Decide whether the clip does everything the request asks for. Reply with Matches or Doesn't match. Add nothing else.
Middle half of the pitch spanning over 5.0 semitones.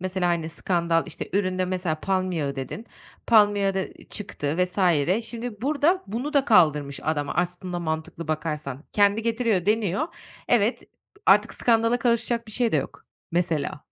Matches